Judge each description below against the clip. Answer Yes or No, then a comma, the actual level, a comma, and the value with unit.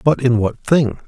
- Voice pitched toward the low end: Yes, low, 125 Hz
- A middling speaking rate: No, fast, 220 wpm